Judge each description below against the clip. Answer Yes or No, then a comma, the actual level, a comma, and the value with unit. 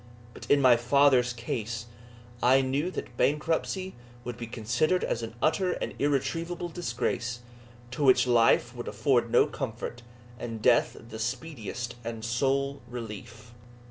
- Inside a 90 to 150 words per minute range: Yes, average, 140 wpm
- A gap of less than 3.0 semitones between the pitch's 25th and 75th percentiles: No, average, 3.3 semitones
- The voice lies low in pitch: Yes, low, 125 Hz